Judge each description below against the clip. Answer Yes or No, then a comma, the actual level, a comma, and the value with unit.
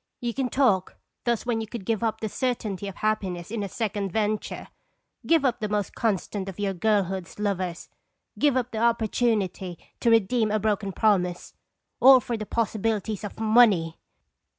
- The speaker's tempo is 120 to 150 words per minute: No, average, 170 wpm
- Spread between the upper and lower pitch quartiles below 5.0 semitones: Yes, average, 3.0 semitones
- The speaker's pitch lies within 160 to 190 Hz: No, high, 215 Hz